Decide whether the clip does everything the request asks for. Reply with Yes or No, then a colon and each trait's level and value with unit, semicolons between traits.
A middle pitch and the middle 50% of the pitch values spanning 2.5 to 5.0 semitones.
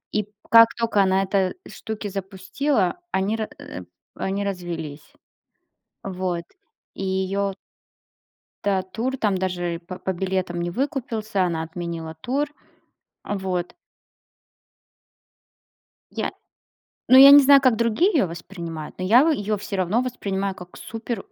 No: high, 195 Hz; average, 3.8 semitones